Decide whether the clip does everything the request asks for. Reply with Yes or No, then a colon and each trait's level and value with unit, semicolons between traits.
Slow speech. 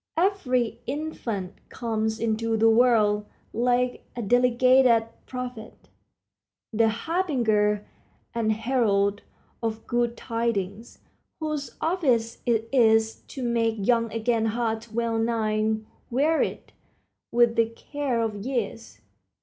Yes: slow, 105 wpm